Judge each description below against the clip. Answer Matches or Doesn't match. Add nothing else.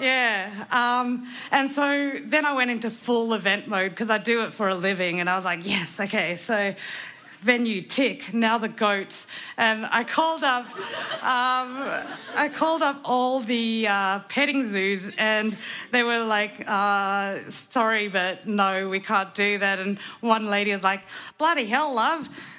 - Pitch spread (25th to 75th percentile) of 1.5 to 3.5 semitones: Doesn't match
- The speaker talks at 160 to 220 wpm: Matches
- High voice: Matches